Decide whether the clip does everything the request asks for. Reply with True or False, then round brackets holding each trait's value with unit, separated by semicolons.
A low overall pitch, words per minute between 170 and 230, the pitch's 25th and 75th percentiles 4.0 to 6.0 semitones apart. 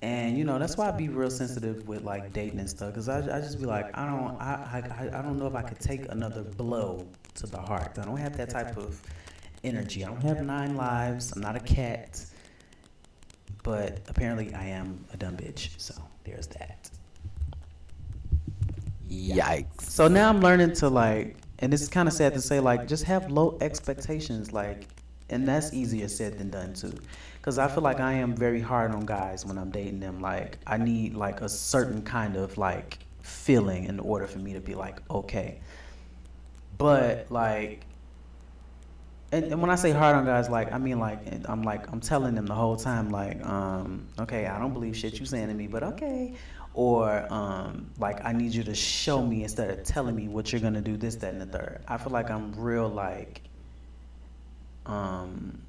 True (105 Hz; 200 wpm; 5.0 semitones)